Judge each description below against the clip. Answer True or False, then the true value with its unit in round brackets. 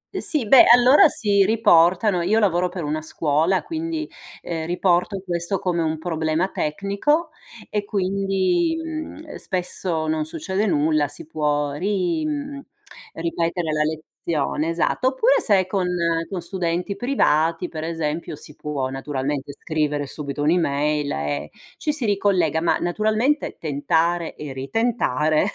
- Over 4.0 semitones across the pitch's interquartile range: True (4.9 semitones)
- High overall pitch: False (175 Hz)